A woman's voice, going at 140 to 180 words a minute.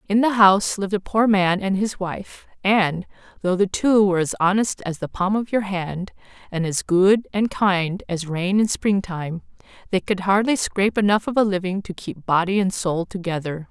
No: female; fast, 205 wpm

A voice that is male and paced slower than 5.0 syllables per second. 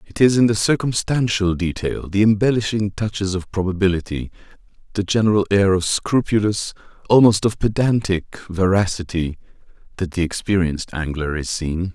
No: male; 5.2 syllables/s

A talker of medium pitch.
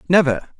Yes: medium, 150 Hz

